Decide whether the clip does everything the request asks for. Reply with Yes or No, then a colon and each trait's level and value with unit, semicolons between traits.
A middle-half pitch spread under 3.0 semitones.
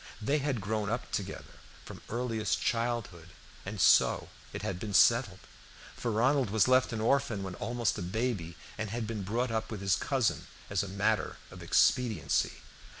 No: average, 3.5 semitones